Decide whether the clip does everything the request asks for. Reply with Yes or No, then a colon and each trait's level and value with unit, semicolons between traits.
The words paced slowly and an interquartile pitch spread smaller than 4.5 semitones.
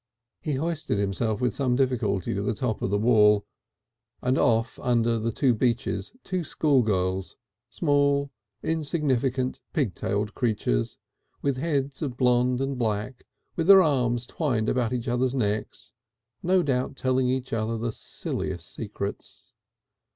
No: average, 145 wpm; average, 3.9 semitones